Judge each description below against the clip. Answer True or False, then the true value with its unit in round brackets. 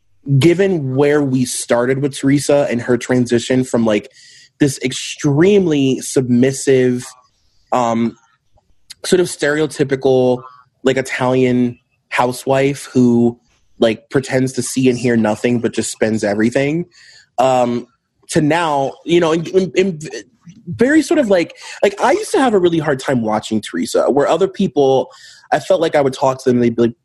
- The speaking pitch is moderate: False (130 Hz)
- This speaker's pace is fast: False (160 wpm)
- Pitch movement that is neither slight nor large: True (3.4 semitones)